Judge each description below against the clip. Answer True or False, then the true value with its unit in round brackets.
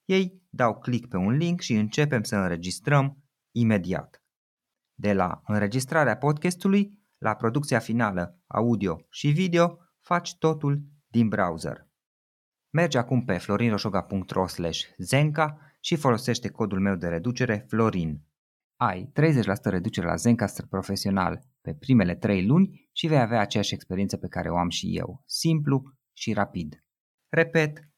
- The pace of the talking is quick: False (135 wpm)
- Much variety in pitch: True (7.0 semitones)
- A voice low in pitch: True (120 Hz)